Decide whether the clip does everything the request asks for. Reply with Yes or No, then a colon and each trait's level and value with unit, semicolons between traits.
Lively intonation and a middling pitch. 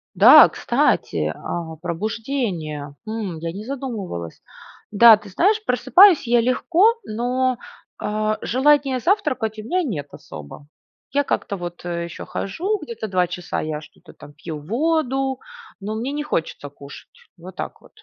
No: wide, 7.7 semitones; high, 220 Hz